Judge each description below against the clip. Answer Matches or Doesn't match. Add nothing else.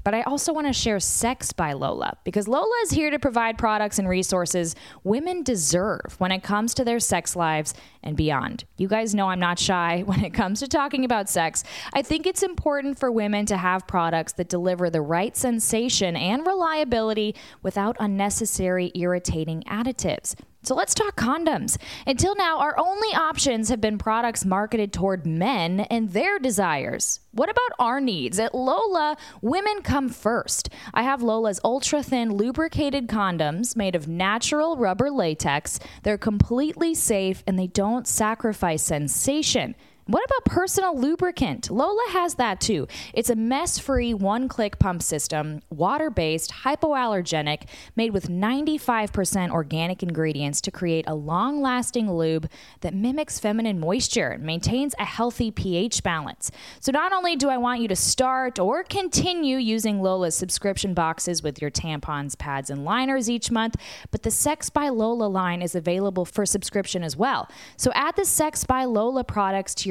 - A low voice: Doesn't match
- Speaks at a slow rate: Doesn't match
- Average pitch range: Doesn't match